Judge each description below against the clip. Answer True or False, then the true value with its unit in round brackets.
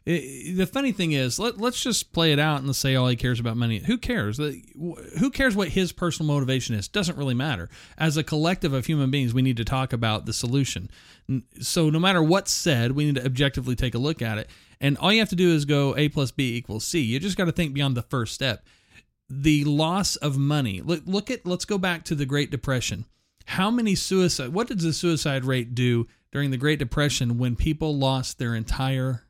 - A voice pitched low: False (145 Hz)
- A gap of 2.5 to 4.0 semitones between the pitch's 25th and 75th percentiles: False (5.2 semitones)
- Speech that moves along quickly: True (225 wpm)